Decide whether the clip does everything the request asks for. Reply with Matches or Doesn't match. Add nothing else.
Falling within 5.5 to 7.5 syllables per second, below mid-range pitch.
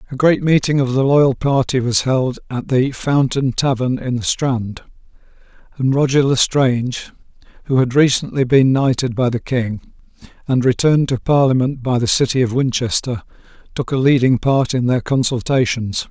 Doesn't match